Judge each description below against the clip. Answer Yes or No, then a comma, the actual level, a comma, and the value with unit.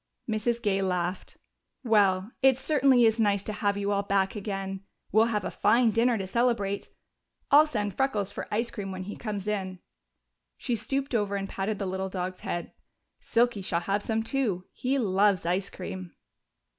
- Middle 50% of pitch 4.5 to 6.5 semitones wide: No, average, 3.2 semitones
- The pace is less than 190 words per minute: Yes, average, 175 wpm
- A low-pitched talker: No, high, 205 Hz